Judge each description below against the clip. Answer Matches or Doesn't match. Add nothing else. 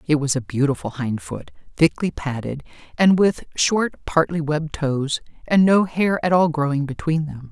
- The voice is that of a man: Doesn't match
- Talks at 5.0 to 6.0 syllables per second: Doesn't match